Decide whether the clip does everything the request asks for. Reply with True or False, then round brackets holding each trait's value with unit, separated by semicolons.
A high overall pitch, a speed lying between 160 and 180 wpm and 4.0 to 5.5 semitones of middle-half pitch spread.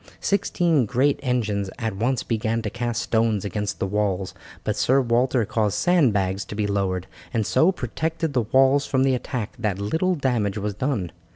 False (115 Hz; 175 wpm; 4.4 semitones)